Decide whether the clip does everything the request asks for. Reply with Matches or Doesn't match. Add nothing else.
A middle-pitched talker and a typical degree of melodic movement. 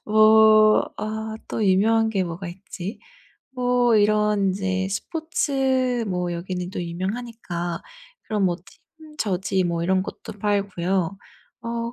Doesn't match